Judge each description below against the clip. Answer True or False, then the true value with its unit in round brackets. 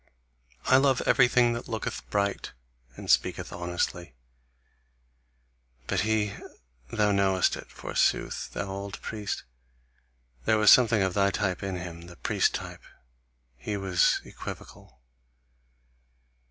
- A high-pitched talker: False (100 Hz)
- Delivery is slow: True (115 wpm)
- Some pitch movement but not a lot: True (3.2 semitones)